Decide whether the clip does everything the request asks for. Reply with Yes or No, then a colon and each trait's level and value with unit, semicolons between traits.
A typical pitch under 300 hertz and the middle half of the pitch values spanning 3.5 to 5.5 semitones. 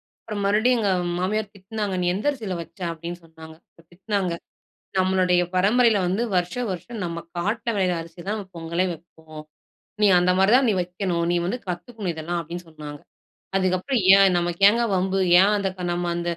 No: medium, 185 Hz; average, 3.1 semitones